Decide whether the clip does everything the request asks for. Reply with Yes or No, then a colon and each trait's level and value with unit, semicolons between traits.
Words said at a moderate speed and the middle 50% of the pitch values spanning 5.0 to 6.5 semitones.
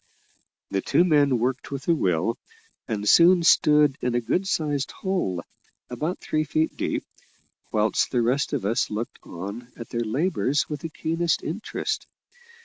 Yes: average, 155 wpm; wide, 5.6 semitones